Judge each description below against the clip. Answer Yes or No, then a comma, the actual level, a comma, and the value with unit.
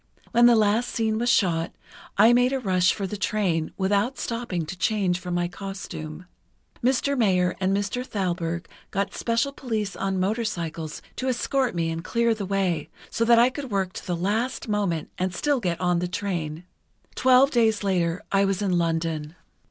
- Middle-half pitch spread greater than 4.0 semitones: Yes, average, 4.7 semitones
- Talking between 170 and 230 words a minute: Yes, average, 175 wpm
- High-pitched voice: Yes, high, 195 Hz